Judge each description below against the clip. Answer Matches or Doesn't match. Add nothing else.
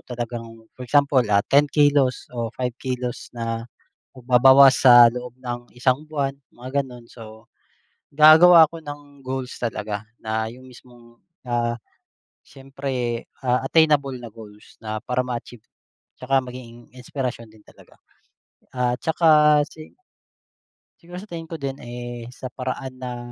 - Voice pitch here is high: Doesn't match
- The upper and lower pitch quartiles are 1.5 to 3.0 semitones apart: Matches